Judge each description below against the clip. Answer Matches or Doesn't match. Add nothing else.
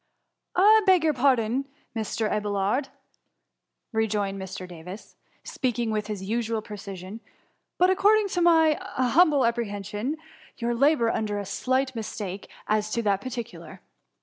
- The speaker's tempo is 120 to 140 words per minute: Matches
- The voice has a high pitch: Matches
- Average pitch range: Matches